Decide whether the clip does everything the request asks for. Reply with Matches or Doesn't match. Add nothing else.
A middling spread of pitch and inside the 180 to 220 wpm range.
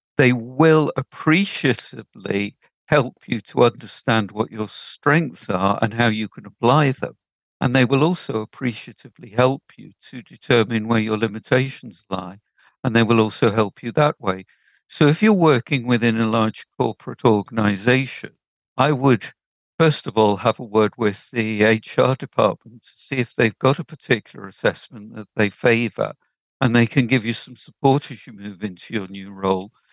Doesn't match